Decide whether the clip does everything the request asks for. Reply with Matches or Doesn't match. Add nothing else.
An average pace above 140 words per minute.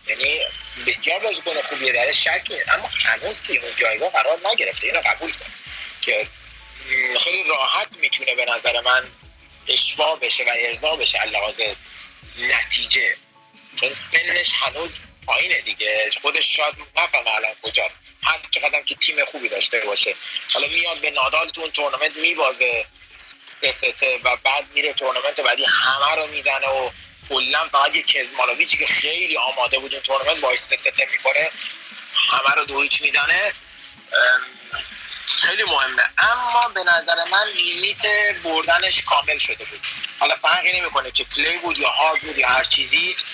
Matches